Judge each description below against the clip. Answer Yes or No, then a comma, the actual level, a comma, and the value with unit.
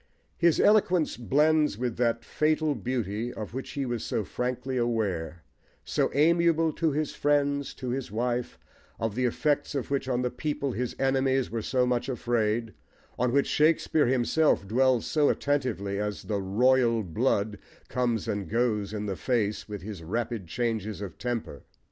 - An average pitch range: Yes, average, 4.3 semitones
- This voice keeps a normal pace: Yes, average, 160 wpm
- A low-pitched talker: Yes, low, 125 Hz